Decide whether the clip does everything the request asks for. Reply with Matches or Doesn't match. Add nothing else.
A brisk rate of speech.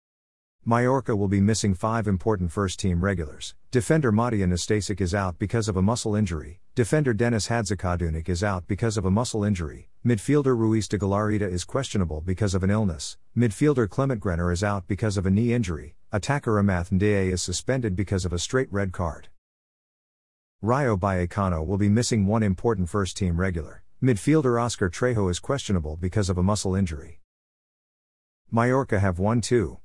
Doesn't match